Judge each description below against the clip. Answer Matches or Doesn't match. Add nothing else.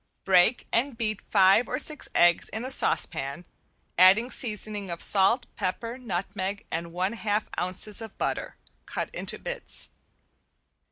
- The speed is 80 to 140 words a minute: Matches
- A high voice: Matches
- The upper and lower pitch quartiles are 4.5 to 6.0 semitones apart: Doesn't match